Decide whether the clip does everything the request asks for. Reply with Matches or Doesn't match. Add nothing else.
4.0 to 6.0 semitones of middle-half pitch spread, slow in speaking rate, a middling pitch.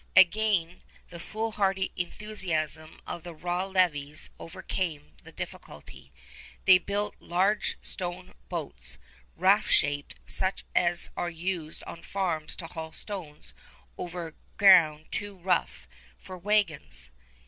Doesn't match